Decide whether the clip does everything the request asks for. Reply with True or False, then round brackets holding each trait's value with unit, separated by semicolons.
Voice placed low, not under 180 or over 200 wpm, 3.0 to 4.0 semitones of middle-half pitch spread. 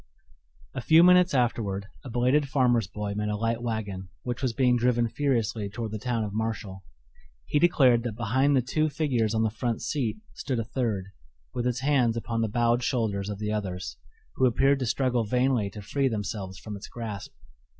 True (115 Hz; 190 wpm; 3.4 semitones)